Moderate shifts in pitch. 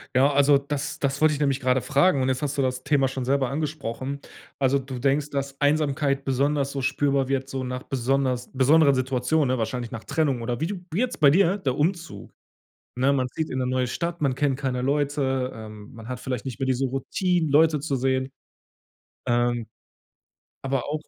No: narrow, 2.2 semitones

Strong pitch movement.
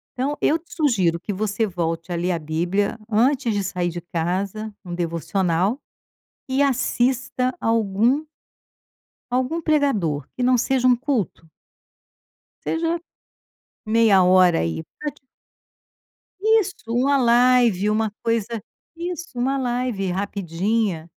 Yes: wide, 6.0 semitones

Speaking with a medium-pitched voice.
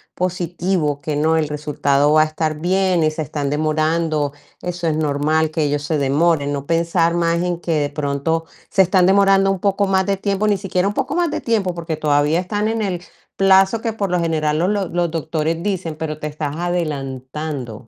Yes: medium, 165 Hz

